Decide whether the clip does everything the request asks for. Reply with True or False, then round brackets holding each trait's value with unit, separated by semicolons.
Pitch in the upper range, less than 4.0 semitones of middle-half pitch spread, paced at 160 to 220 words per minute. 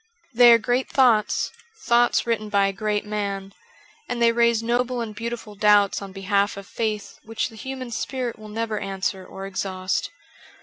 True (215 Hz; 2.9 semitones; 170 wpm)